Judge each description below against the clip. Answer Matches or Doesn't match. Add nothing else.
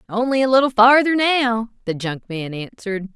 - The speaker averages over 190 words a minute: Doesn't match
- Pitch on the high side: Matches